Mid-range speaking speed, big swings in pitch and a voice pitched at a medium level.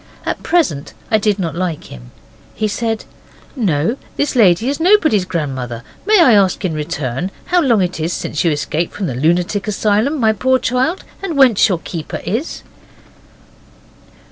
No: average, 165 wpm; wide, 7.4 semitones; high, 200 Hz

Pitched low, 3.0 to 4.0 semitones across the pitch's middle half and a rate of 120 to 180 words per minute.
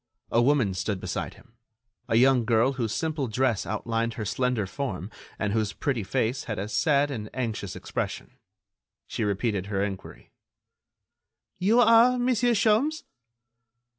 No: low, 120 Hz; wide, 5.5 semitones; average, 140 wpm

